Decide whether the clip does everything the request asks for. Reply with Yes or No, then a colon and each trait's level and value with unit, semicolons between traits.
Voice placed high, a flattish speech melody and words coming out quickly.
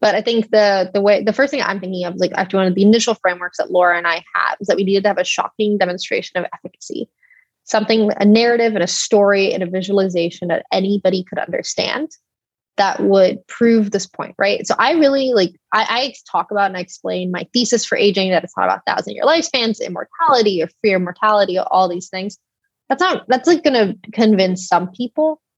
No: high, 200 Hz; average, 3.7 semitones; fast, 215 wpm